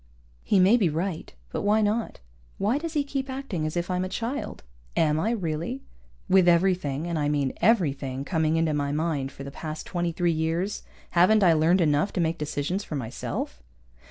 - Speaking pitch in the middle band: Yes, medium, 170 Hz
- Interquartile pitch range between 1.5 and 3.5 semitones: No, average, 4.6 semitones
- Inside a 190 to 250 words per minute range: Yes, average, 195 wpm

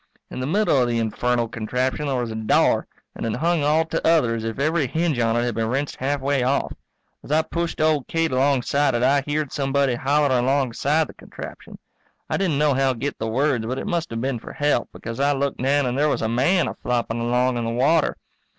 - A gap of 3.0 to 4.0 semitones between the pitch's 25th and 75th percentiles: Yes, average, 3.6 semitones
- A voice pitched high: No, low, 135 Hz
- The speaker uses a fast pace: Yes, fast, 225 wpm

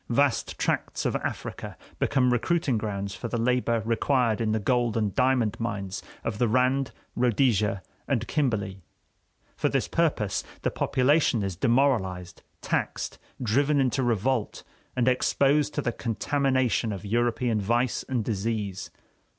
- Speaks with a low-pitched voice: Yes, low, 120 Hz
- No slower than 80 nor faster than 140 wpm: Yes, slow, 135 wpm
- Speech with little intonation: No, average, 3.4 semitones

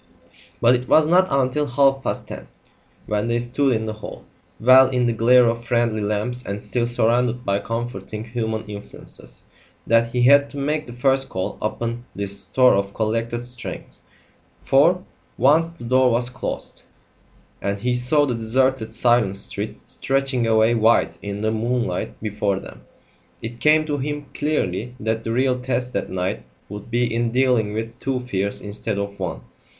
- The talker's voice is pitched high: No, low, 120 Hz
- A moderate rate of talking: Yes, average, 170 wpm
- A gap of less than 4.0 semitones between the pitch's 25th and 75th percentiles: Yes, average, 2.8 semitones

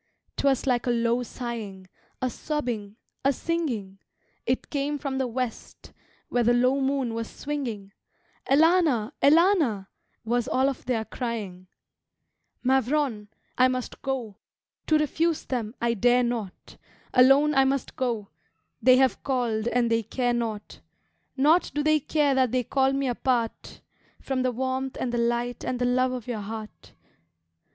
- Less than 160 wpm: Yes, average, 150 wpm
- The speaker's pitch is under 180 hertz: No, very high, 250 Hz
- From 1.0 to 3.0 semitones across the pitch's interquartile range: Yes, average, 2.7 semitones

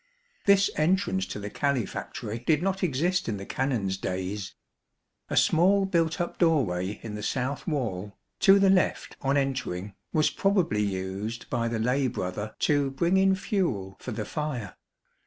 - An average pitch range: No, wide, 8.6 semitones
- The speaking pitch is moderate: No, low, 130 Hz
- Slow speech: No, average, 155 wpm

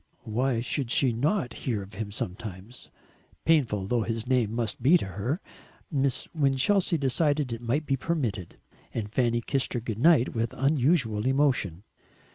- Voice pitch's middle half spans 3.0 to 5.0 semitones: Yes, average, 4.0 semitones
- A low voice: Yes, low, 125 Hz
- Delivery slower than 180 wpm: Yes, average, 155 wpm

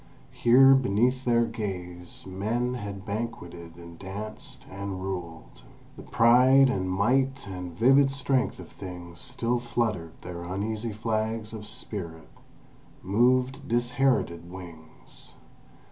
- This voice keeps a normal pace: No, slow, 115 wpm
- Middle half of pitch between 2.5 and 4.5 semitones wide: No, average, 5.3 semitones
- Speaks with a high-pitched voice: No, low, 105 Hz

